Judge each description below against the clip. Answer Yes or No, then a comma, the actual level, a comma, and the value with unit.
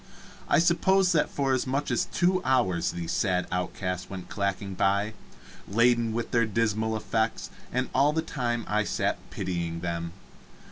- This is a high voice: No, low, 110 Hz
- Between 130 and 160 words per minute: Yes, average, 155 wpm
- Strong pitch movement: Yes, wide, 5.9 semitones